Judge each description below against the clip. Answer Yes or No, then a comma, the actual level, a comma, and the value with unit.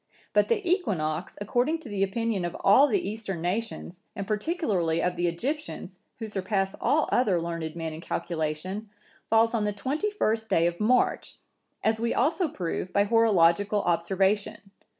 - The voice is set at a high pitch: Yes, high, 205 Hz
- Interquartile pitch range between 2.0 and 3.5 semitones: No, average, 4.8 semitones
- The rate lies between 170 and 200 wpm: No, average, 160 wpm